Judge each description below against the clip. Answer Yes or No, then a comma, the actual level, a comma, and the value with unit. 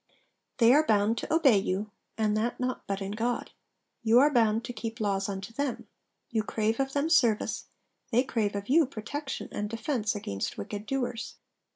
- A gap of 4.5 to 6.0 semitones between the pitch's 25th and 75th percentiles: No, average, 3.5 semitones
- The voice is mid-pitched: No, high, 225 Hz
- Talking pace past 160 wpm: Yes, average, 180 wpm